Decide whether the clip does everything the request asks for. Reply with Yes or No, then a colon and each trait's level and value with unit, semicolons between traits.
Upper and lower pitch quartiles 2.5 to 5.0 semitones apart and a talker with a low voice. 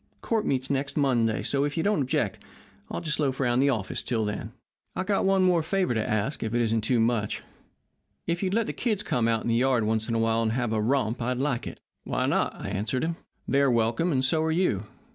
No: wide, 5.6 semitones; low, 130 Hz